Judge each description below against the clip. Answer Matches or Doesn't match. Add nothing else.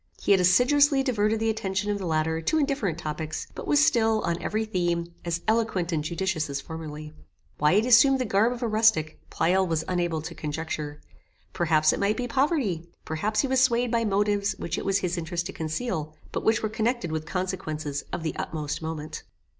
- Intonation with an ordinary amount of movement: Doesn't match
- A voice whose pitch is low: Doesn't match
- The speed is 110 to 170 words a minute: Doesn't match